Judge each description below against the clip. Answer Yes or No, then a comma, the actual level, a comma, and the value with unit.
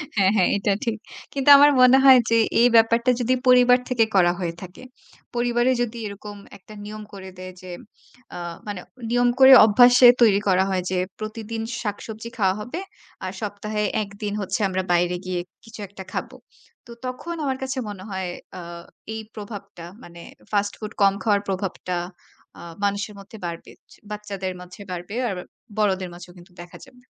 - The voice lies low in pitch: No, high, 205 Hz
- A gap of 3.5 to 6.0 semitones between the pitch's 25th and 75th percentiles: Yes, average, 3.9 semitones